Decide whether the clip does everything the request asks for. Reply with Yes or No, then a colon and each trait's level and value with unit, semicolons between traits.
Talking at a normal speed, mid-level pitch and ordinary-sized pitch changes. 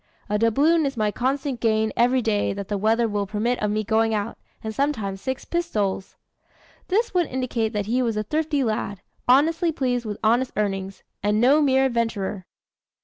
No: average, 180 wpm; high, 230 Hz; average, 4.1 semitones